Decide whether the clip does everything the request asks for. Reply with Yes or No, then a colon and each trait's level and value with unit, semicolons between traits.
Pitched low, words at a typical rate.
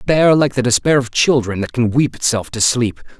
No: low, 125 Hz; fast, 225 wpm